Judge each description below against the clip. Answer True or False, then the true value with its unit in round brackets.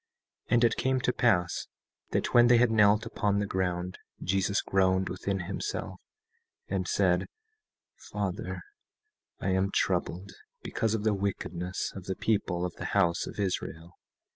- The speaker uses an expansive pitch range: False (3.3 semitones)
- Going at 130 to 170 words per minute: True (150 wpm)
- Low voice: True (100 Hz)